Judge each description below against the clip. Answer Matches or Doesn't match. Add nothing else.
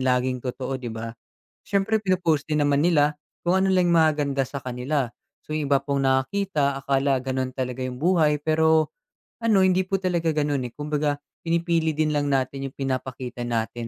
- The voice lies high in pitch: Doesn't match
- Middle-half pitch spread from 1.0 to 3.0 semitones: Doesn't match